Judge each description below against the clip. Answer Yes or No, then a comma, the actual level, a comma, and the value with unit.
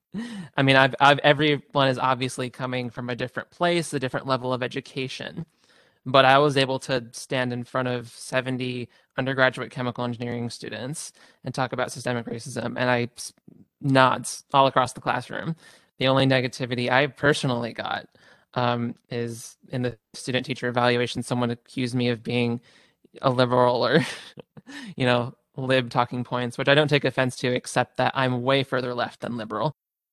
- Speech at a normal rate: Yes, average, 165 wpm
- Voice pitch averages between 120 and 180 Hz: Yes, low, 130 Hz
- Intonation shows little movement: Yes, narrow, 1.6 semitones